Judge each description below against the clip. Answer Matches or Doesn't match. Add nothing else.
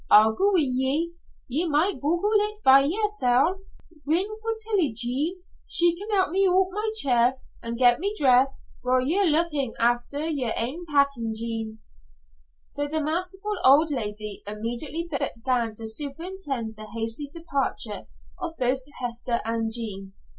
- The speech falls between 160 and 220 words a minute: Doesn't match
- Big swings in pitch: Matches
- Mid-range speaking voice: Doesn't match